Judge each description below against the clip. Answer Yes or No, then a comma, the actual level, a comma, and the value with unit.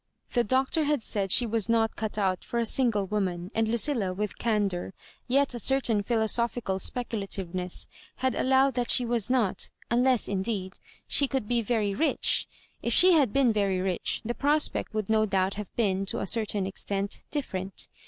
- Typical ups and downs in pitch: Yes, average, 4.0 semitones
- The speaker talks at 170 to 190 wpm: Yes, average, 180 wpm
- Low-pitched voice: No, high, 220 Hz